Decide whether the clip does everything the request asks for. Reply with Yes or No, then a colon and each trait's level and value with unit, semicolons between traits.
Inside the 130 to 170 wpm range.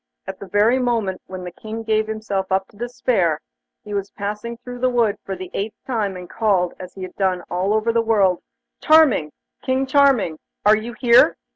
No: average, 195 wpm